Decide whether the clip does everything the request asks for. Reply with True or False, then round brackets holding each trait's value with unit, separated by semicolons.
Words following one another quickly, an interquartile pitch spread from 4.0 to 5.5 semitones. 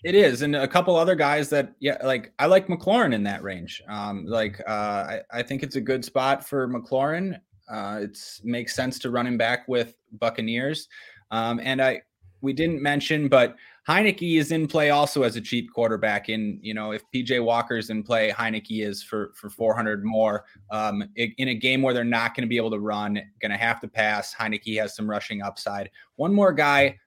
True (210 wpm; 4.3 semitones)